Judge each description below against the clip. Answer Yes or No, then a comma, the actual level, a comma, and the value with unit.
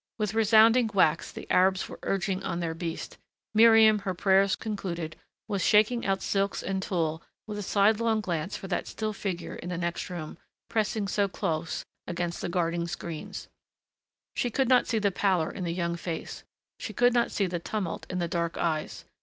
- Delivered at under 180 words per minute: No, average, 185 wpm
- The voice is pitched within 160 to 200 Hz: Yes, high, 190 Hz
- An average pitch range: Yes, average, 3.9 semitones